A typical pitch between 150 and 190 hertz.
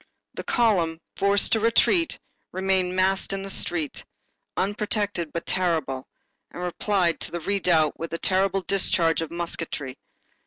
Yes: medium, 185 Hz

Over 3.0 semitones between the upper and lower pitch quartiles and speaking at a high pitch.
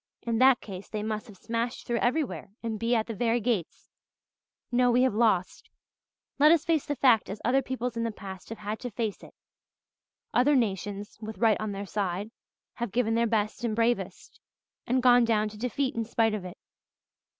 No: average, 2.7 semitones; high, 230 Hz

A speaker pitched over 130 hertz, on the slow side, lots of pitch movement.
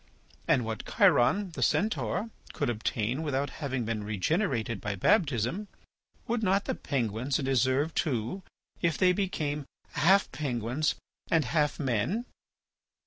Yes: medium, 140 Hz; slow, 125 wpm; wide, 6.6 semitones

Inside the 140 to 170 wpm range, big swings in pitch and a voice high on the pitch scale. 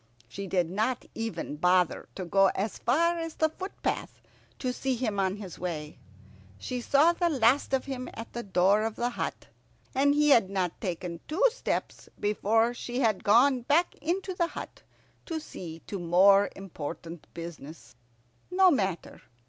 Yes: average, 165 wpm; wide, 7.2 semitones; high, 220 Hz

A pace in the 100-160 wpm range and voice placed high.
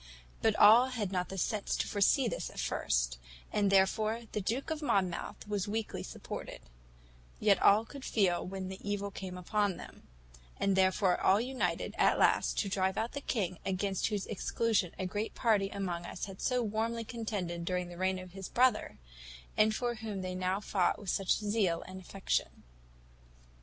No: average, 180 wpm; high, 200 Hz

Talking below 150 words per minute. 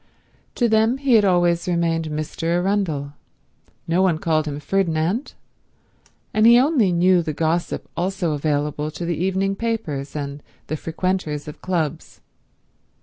Yes: average, 140 wpm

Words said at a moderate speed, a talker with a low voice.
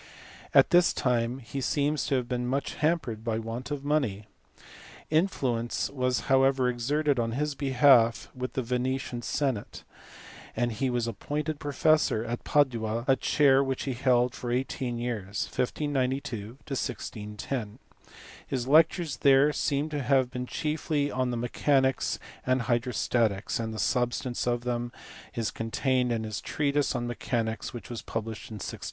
Yes: average, 145 wpm; low, 125 Hz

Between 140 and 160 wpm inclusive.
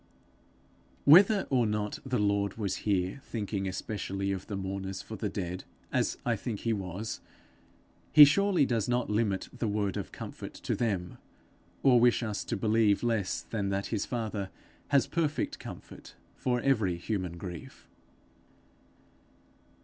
Yes: average, 145 wpm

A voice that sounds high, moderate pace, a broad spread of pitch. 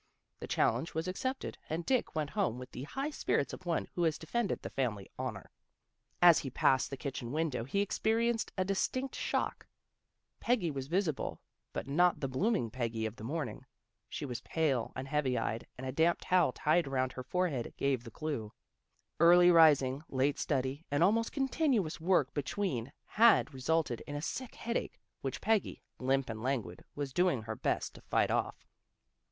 No: medium, 150 Hz; average, 180 wpm; wide, 5.8 semitones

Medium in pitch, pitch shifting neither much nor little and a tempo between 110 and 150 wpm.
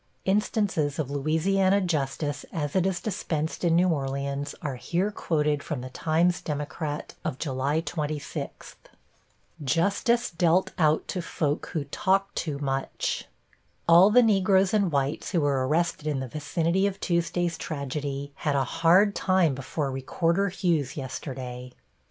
Yes: medium, 160 Hz; average, 4.6 semitones; average, 140 wpm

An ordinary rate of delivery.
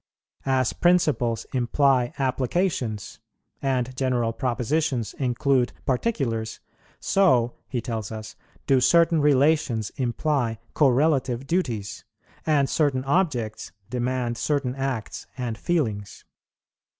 No: slow, 95 wpm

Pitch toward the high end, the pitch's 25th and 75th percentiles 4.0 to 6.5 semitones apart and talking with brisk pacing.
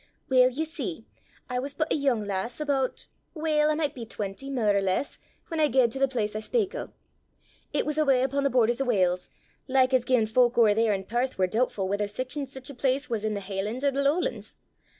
Yes: very high, 255 Hz; average, 4.5 semitones; fast, 230 wpm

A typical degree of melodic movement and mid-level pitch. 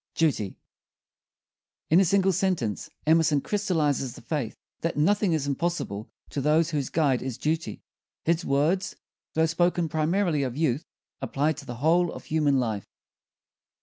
Yes: average, 3.5 semitones; medium, 155 Hz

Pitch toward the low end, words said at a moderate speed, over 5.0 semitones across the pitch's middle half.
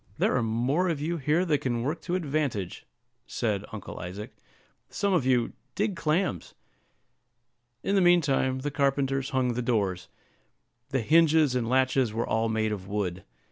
Yes: low, 130 Hz; average, 165 wpm; wide, 5.6 semitones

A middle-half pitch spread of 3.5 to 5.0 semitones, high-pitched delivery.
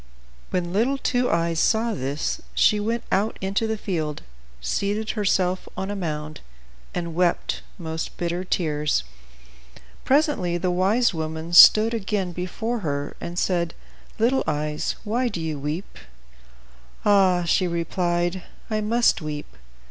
No: average, 4.5 semitones; medium, 180 Hz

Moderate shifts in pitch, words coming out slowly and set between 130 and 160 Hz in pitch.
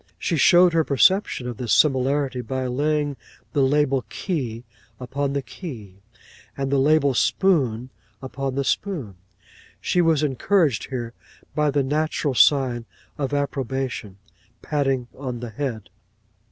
Yes: average, 3.0 semitones; slow, 130 wpm; low, 135 Hz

